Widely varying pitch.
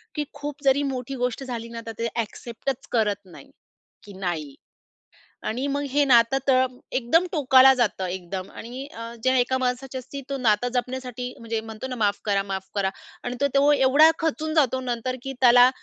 No: average, 3.0 semitones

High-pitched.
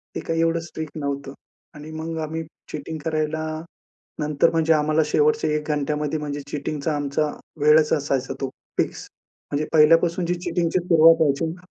No: medium, 155 Hz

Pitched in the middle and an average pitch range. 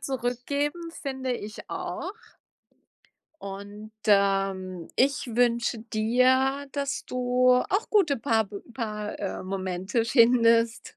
No: high, 235 Hz; average, 4.1 semitones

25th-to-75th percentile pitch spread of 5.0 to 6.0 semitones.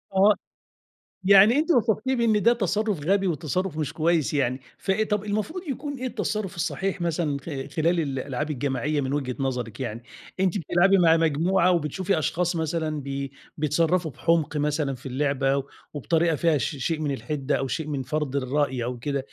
Yes: average, 5.3 semitones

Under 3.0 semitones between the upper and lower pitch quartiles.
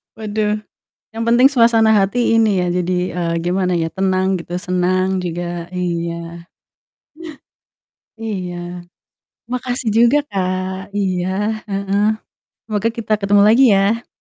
No: average, 3.5 semitones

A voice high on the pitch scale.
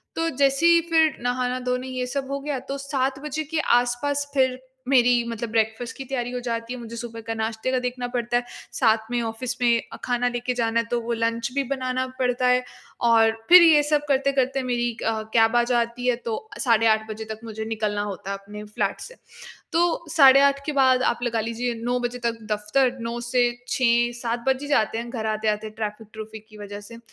Yes: high, 240 Hz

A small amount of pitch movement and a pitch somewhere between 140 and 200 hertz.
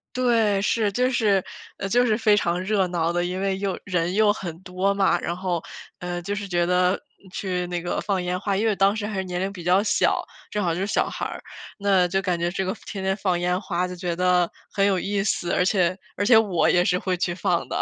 Yes: narrow, 2.2 semitones; high, 190 Hz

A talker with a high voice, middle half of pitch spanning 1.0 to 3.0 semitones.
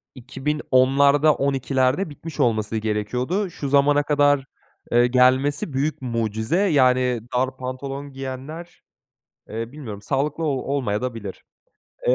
No: low, 135 Hz; average, 2.7 semitones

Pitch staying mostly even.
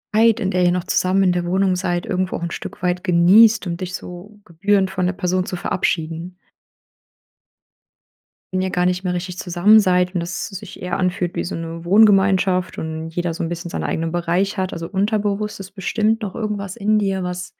Yes: narrow, 2.0 semitones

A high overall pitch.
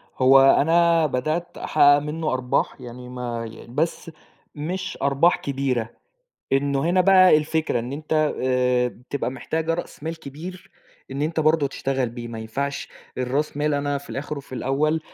No: medium, 140 Hz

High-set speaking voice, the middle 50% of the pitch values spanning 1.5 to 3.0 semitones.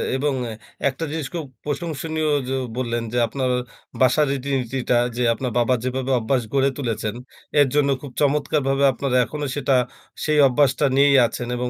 No: low, 135 Hz; narrow, 2.5 semitones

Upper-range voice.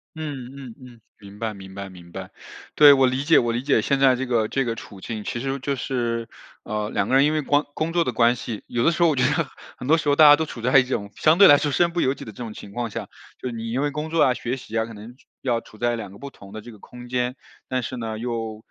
No: low, 125 Hz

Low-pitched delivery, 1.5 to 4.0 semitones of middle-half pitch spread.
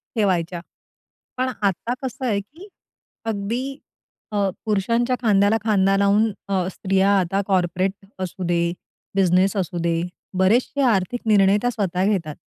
No: high, 200 Hz; average, 3.1 semitones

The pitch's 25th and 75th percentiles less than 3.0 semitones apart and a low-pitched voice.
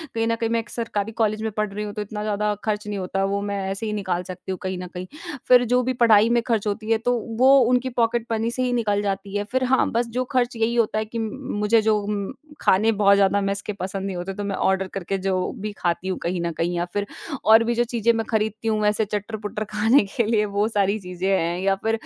No: narrow, 2.5 semitones; high, 210 Hz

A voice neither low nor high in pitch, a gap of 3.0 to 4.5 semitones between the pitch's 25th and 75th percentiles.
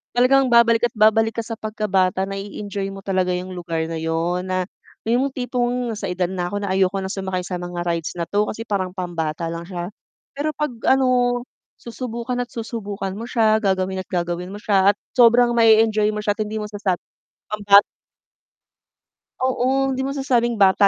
No: high, 205 Hz; average, 4.2 semitones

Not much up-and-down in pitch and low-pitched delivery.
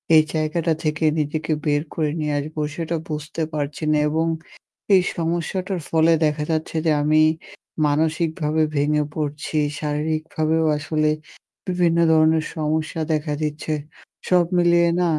No: narrow, 1.4 semitones; medium, 155 Hz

